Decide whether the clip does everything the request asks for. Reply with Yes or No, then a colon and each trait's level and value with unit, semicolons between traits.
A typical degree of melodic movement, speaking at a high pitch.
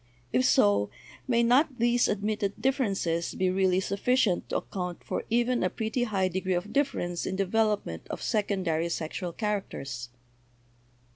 Yes: average, 4.6 semitones; high, 195 Hz